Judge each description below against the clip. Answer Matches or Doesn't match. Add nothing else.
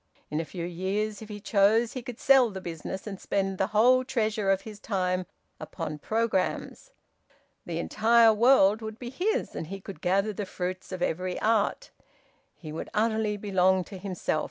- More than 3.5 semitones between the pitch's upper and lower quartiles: Doesn't match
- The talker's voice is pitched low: Doesn't match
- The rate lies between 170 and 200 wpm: Matches